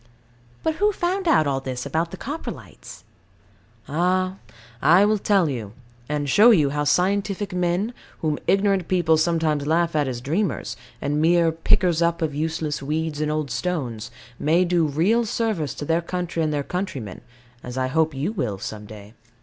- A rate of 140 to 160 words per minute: No, average, 170 wpm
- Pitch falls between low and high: Yes, medium, 160 Hz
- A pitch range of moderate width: Yes, average, 4.3 semitones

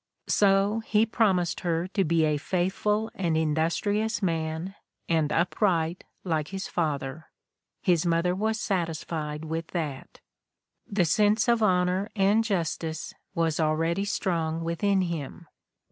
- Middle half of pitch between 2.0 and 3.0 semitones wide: No, average, 3.7 semitones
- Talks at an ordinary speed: No, slow, 125 wpm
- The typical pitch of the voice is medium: Yes, medium, 175 Hz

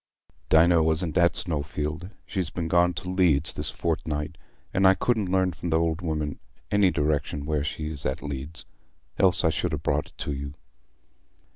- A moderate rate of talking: Yes, average, 170 wpm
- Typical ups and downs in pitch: Yes, average, 3.0 semitones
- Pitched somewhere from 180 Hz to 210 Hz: No, very low, 80 Hz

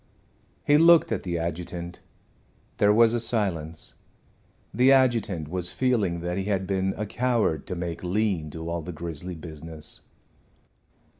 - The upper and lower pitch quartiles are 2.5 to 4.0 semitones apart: No, average, 4.7 semitones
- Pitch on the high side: No, very low, 90 Hz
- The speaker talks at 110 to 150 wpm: Yes, average, 145 wpm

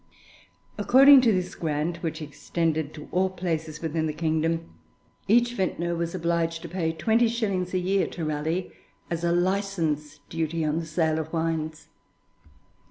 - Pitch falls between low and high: Yes, medium, 165 Hz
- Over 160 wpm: No, average, 155 wpm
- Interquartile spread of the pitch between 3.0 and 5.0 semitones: No, narrow, 2.6 semitones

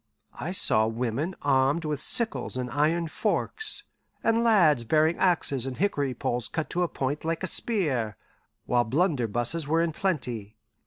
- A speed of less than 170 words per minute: Yes, average, 155 wpm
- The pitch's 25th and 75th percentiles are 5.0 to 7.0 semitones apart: Yes, wide, 5.5 semitones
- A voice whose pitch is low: No, medium, 150 Hz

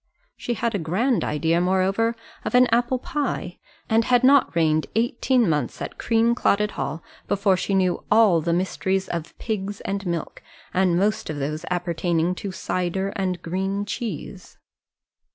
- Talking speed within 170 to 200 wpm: No, average, 150 wpm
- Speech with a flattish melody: No, average, 4.5 semitones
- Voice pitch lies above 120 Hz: Yes, high, 190 Hz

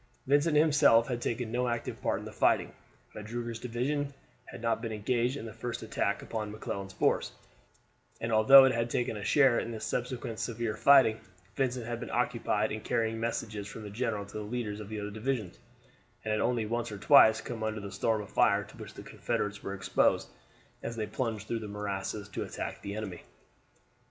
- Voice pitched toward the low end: Yes, low, 115 Hz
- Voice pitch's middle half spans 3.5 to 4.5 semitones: No, narrow, 2.4 semitones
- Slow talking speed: No, average, 200 wpm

